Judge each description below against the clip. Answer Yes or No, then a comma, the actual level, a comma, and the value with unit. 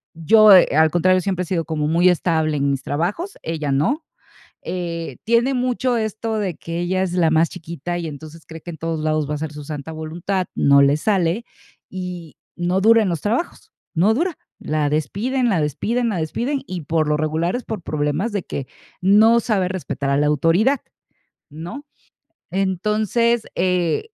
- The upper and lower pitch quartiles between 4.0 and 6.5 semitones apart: Yes, average, 5.3 semitones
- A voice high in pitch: No, medium, 175 Hz